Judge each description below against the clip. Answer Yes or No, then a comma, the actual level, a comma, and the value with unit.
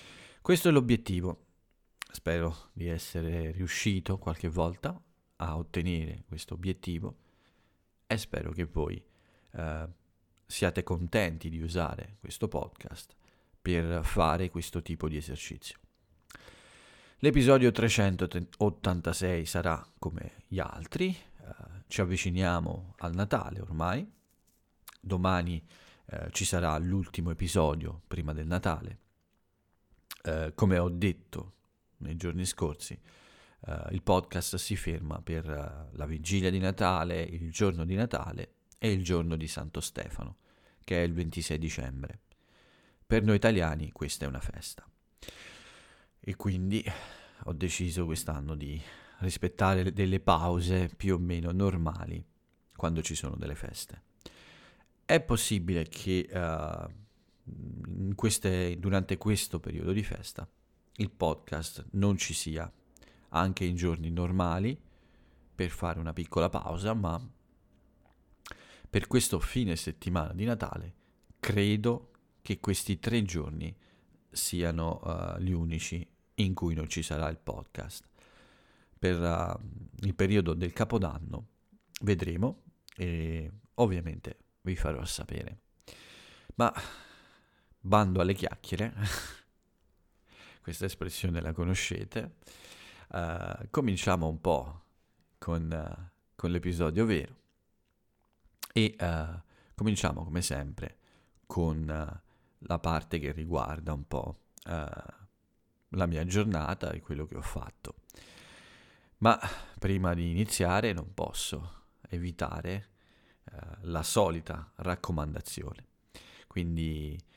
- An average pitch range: Yes, average, 3.2 semitones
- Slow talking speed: Yes, slow, 110 wpm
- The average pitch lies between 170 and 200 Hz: No, very low, 90 Hz